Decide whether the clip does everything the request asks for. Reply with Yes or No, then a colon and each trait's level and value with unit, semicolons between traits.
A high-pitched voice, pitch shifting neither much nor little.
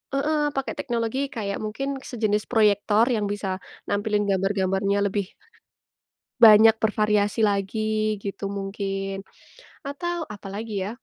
No: high, 210 Hz; narrow, 2.2 semitones